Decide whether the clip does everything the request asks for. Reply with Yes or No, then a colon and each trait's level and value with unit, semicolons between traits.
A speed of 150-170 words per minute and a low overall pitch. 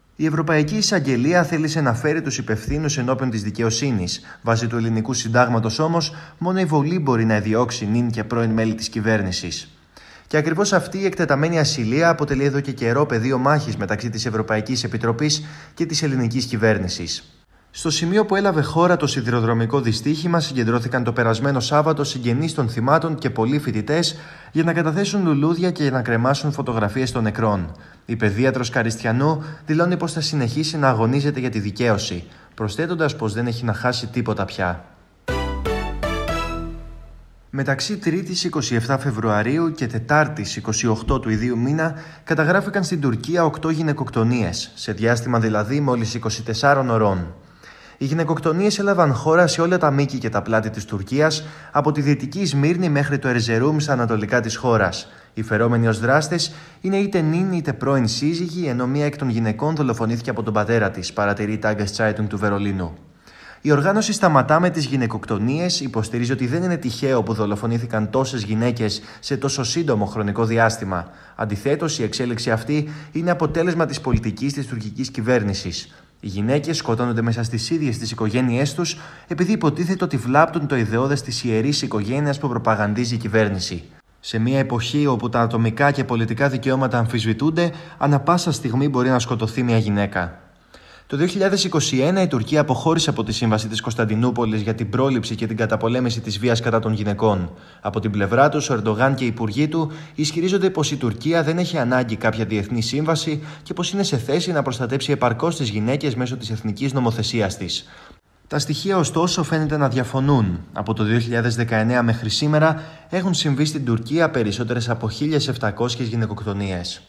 Yes: average, 160 wpm; low, 125 Hz